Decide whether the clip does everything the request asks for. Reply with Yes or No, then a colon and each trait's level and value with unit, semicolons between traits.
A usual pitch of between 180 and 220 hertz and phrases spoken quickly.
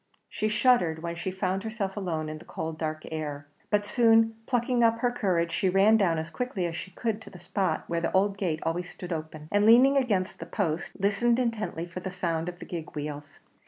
Yes: medium, 185 Hz; fast, 220 wpm